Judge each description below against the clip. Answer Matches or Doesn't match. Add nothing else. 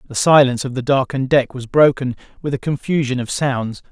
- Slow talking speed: Doesn't match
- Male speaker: Matches